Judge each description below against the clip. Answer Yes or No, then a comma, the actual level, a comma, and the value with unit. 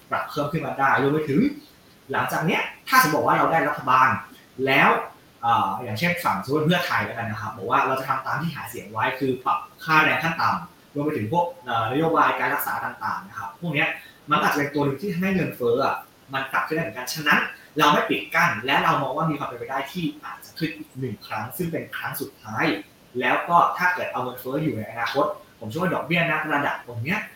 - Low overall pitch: No, medium, 150 Hz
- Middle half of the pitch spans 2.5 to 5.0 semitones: Yes, average, 3.7 semitones